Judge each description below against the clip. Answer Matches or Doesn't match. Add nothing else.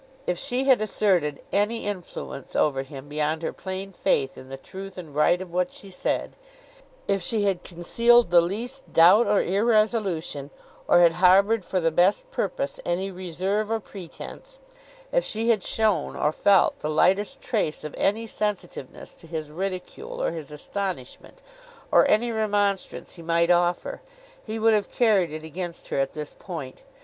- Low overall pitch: Doesn't match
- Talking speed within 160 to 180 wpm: Matches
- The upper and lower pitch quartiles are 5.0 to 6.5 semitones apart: Doesn't match